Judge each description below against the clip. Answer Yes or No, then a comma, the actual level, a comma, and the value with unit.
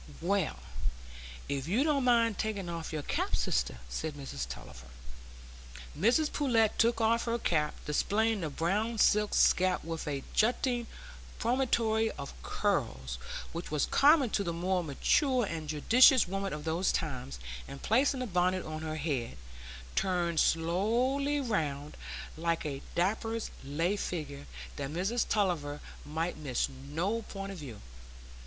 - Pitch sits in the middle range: Yes, medium, 180 Hz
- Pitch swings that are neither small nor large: No, wide, 7.0 semitones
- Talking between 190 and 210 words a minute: No, average, 140 wpm